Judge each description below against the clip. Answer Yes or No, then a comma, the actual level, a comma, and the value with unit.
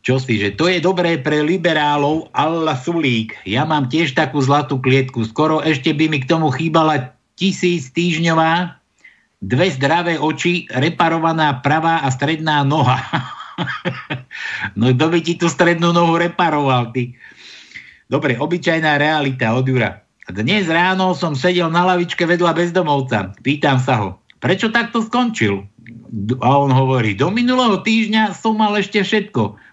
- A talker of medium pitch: Yes, medium, 155 Hz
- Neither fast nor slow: Yes, average, 145 wpm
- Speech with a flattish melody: No, average, 4.9 semitones